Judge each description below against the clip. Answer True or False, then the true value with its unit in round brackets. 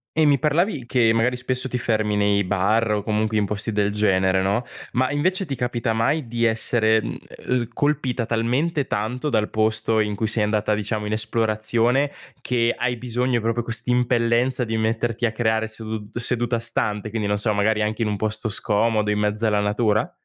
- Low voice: True (115 Hz)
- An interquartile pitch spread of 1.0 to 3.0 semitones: True (2.4 semitones)